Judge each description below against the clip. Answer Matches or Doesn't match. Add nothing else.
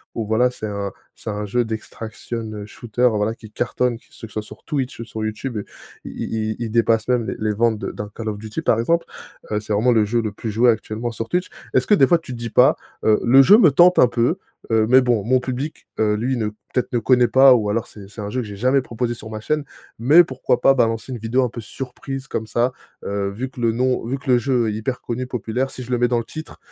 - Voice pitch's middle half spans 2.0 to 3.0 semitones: Matches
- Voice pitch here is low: Matches